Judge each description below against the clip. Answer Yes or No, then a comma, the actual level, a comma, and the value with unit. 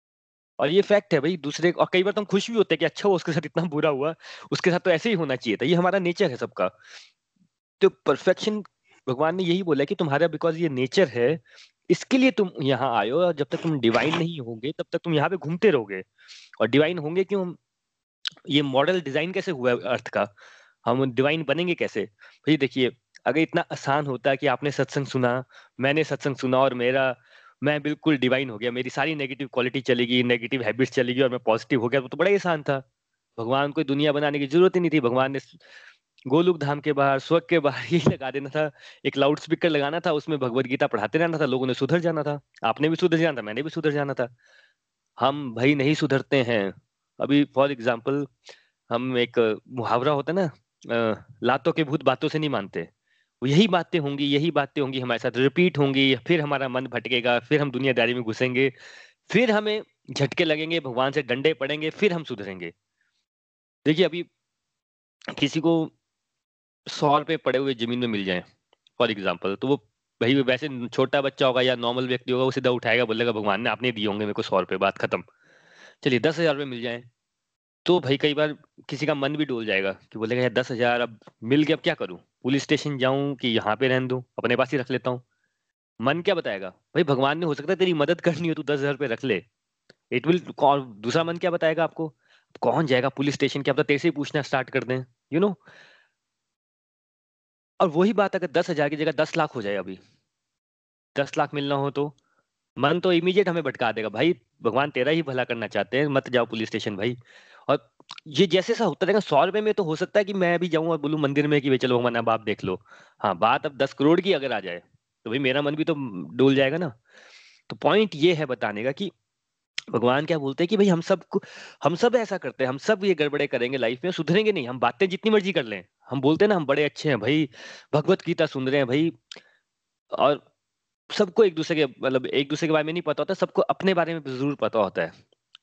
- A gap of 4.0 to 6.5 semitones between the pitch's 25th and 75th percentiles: Yes, average, 4.6 semitones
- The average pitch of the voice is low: No, medium, 145 Hz